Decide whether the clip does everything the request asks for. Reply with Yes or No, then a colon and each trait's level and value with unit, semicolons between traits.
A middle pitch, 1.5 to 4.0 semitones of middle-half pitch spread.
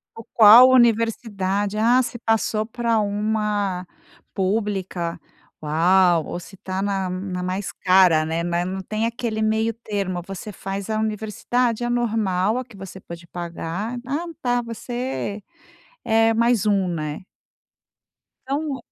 No: high, 210 Hz; average, 3.5 semitones